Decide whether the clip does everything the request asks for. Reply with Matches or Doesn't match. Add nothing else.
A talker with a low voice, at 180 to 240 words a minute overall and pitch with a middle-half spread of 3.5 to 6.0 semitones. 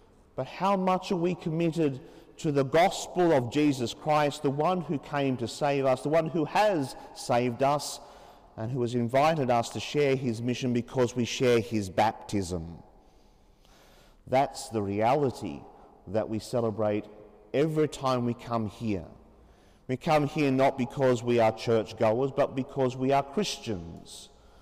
Doesn't match